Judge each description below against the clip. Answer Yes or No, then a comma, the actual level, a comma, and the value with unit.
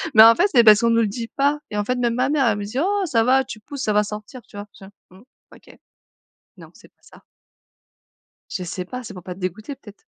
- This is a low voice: No, high, 230 Hz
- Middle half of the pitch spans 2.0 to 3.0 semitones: No, average, 3.8 semitones